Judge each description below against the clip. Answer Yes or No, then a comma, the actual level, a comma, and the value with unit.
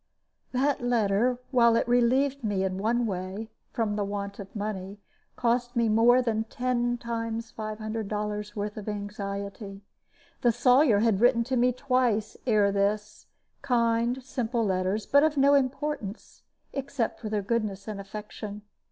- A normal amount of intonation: Yes, average, 3.0 semitones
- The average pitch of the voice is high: Yes, high, 225 Hz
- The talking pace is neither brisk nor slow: Yes, average, 150 wpm